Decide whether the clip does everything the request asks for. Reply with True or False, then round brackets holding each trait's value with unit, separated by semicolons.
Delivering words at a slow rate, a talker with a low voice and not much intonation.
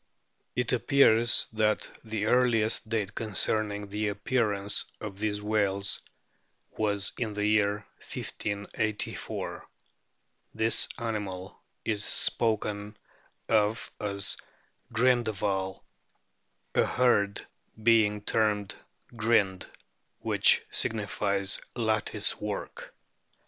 True (85 wpm; 105 Hz; 1.7 semitones)